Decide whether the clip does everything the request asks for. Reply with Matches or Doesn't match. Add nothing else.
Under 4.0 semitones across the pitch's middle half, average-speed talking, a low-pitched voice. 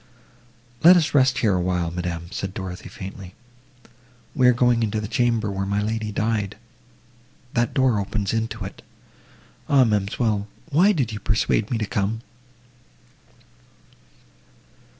Doesn't match